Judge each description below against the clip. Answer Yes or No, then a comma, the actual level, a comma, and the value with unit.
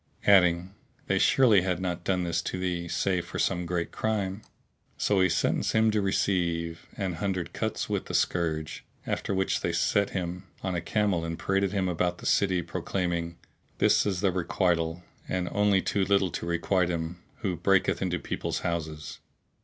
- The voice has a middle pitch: No, very low, 90 Hz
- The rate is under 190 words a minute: Yes, average, 175 wpm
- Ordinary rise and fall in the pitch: No, narrow, 2.1 semitones